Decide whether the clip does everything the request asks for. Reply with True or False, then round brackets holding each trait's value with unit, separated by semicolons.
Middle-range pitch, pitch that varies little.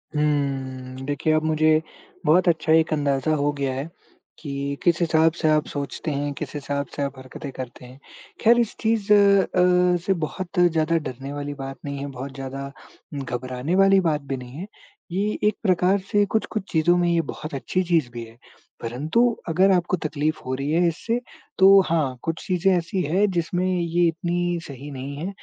False (155 Hz; 4.3 semitones)